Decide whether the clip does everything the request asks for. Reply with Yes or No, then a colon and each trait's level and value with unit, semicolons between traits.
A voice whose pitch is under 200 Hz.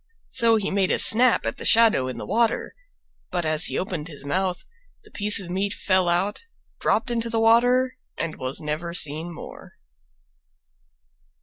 Yes: high, 190 Hz